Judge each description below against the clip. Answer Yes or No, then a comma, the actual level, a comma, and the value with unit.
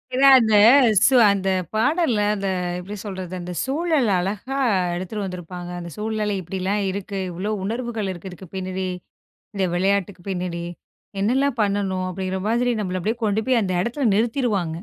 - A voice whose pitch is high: Yes, high, 200 Hz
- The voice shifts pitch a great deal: No, average, 3.6 semitones